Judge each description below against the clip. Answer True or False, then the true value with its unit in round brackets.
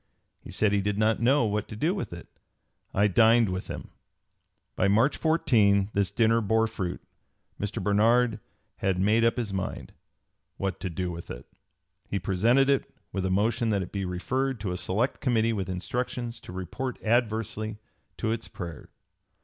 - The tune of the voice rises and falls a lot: False (3.4 semitones)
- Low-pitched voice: True (105 Hz)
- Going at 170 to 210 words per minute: True (175 wpm)